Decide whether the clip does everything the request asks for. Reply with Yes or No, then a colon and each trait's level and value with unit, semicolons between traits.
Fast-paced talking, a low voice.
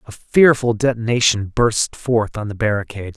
No: average, 150 wpm; low, 110 Hz